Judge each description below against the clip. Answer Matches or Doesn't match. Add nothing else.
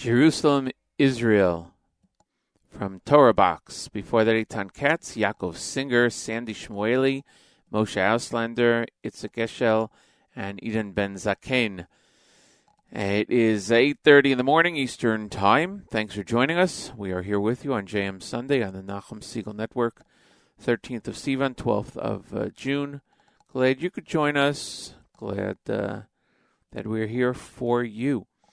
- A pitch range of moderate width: Matches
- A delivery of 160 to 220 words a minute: Doesn't match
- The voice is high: Doesn't match